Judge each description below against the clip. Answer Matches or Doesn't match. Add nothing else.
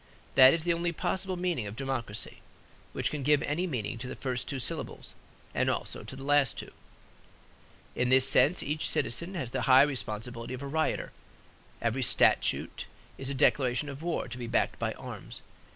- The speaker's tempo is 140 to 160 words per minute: Doesn't match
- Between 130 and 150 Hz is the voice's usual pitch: Matches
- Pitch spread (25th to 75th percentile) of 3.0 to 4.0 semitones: Matches